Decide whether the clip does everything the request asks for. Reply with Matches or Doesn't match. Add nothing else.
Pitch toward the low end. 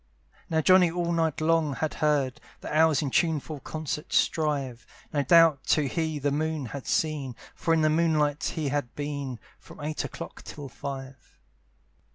Doesn't match